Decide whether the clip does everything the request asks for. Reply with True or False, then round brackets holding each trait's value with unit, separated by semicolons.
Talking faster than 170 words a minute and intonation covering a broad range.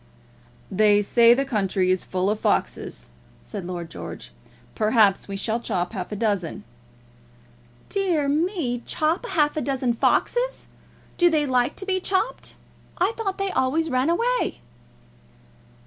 False (140 wpm; 9.0 semitones)